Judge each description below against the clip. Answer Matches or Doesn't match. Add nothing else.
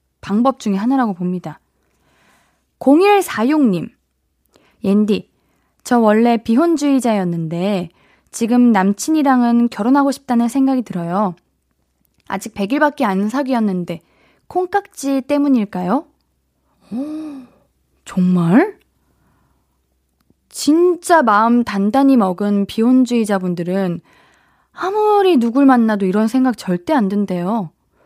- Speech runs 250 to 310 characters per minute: Doesn't match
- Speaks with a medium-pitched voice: Doesn't match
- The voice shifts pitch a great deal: Matches